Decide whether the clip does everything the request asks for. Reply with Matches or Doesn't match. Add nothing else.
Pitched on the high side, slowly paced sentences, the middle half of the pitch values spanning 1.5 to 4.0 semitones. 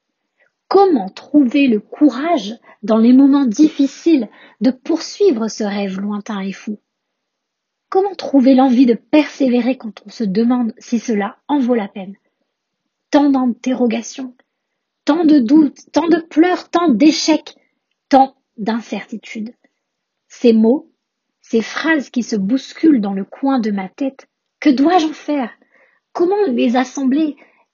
Doesn't match